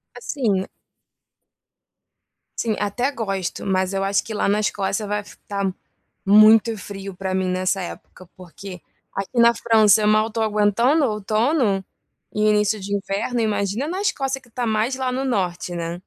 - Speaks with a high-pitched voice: Yes, high, 210 Hz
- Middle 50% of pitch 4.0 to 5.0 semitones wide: No, average, 3.0 semitones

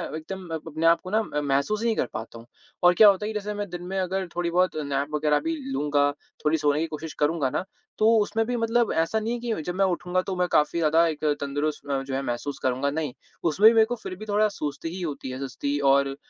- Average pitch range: No, wide, 5.9 semitones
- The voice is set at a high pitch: No, medium, 165 Hz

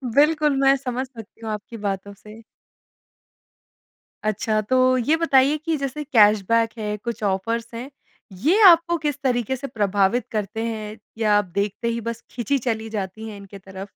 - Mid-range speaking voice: No, high, 230 Hz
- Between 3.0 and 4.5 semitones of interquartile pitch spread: Yes, average, 4.0 semitones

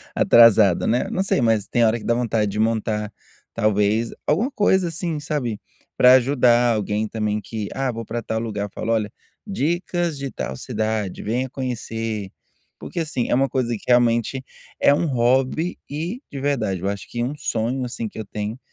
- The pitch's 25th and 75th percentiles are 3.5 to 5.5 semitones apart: Yes, average, 3.9 semitones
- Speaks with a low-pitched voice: Yes, low, 120 Hz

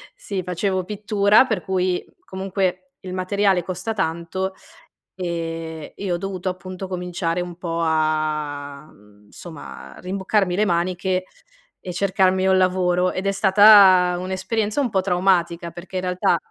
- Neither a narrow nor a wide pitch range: No, narrow, 1.9 semitones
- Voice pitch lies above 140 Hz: Yes, medium, 185 Hz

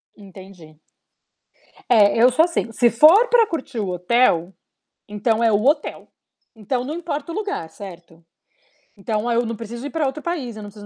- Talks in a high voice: Yes, high, 230 Hz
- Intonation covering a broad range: Yes, wide, 6.1 semitones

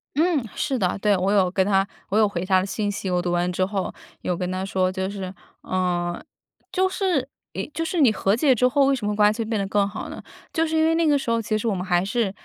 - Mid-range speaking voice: No, high, 205 Hz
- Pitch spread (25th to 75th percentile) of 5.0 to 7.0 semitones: Yes, wide, 5.4 semitones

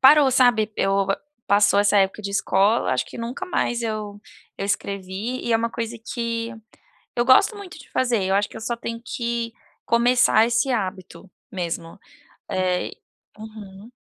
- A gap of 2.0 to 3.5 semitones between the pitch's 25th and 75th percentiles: Yes, average, 3.2 semitones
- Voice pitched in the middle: No, high, 220 Hz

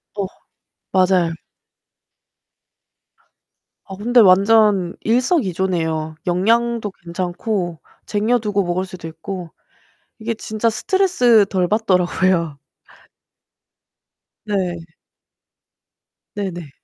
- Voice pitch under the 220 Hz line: Yes, high, 190 Hz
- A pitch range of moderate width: Yes, average, 3.8 semitones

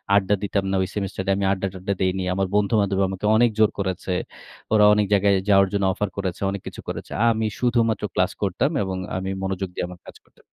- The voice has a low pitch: Yes, low, 100 Hz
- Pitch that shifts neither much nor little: No, narrow, 1.6 semitones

